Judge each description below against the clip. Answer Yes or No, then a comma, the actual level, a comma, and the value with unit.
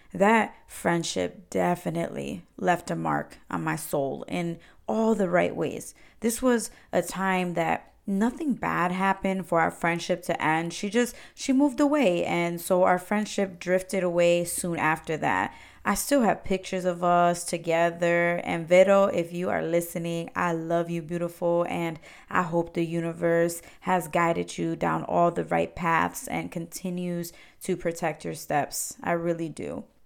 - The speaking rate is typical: Yes, average, 160 wpm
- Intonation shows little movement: Yes, narrow, 2.0 semitones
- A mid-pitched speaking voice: Yes, medium, 175 Hz